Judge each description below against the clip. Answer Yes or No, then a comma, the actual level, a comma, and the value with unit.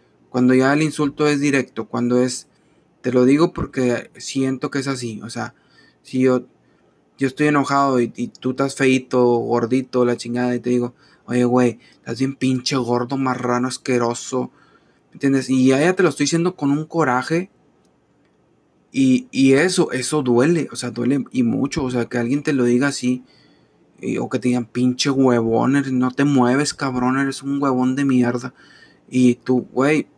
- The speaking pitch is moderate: No, low, 130 Hz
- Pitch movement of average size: No, narrow, 2.3 semitones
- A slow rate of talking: No, average, 180 wpm